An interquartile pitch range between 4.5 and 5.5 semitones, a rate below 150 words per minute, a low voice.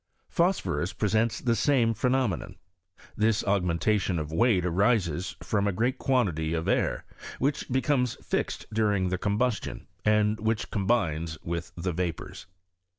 Yes: average, 4.9 semitones; average, 140 wpm; low, 105 Hz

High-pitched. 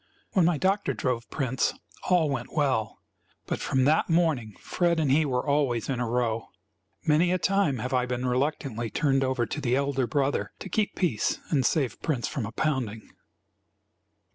No: low, 135 Hz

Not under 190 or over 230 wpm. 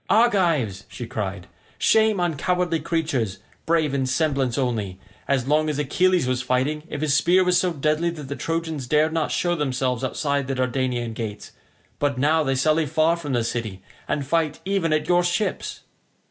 No: average, 175 wpm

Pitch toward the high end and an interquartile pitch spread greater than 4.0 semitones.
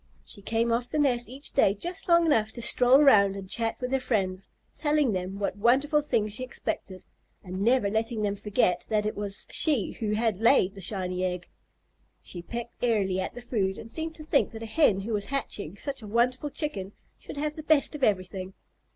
Yes: high, 225 Hz; average, 5.2 semitones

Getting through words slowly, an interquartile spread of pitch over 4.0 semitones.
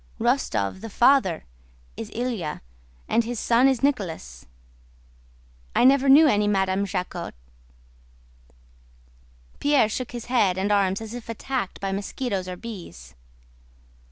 Yes: slow, 125 wpm; average, 4.7 semitones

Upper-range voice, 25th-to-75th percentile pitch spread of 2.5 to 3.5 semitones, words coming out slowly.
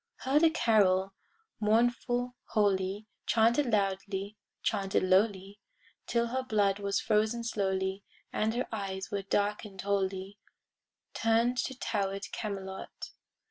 Yes: high, 205 Hz; average, 2.9 semitones; slow, 115 wpm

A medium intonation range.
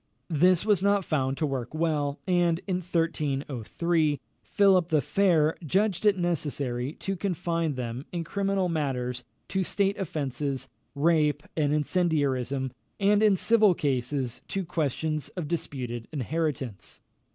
Yes: average, 4.7 semitones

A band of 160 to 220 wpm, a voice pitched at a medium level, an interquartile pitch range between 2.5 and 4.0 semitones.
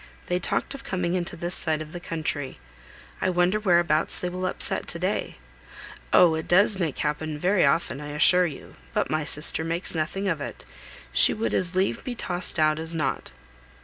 Yes: average, 185 wpm; medium, 170 Hz; average, 2.8 semitones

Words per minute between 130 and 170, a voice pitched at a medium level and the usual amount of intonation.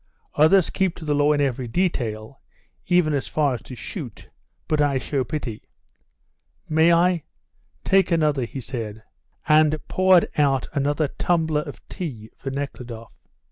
Yes: average, 145 wpm; medium, 145 Hz; average, 3.8 semitones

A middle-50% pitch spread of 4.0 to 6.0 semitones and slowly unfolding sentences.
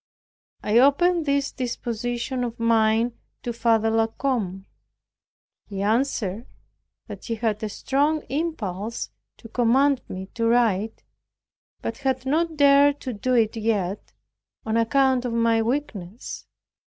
No: average, 3.4 semitones; slow, 125 wpm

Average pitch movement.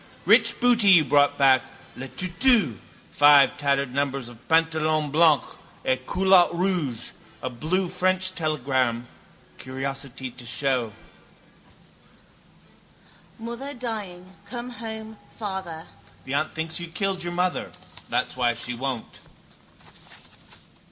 No: wide, 5.9 semitones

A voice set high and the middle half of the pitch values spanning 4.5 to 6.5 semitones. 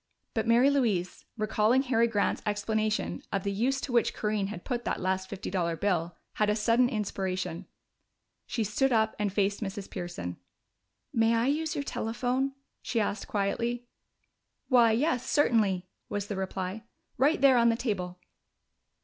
No: high, 215 Hz; average, 3.7 semitones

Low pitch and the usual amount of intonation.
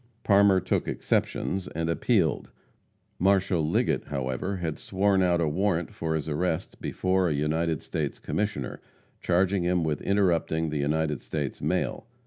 Yes: very low, 85 Hz; average, 3.3 semitones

